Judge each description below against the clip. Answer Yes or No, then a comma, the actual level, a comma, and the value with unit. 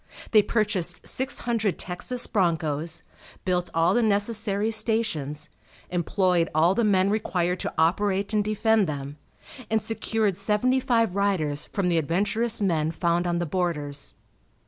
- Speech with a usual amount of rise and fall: Yes, average, 4.3 semitones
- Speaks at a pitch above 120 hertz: Yes, high, 190 Hz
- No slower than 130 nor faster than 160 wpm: Yes, average, 140 wpm